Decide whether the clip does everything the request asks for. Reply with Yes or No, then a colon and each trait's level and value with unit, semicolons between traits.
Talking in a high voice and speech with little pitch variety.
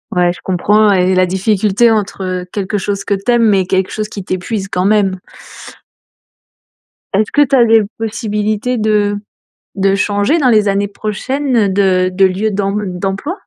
Yes: high, 205 Hz; narrow, 2.2 semitones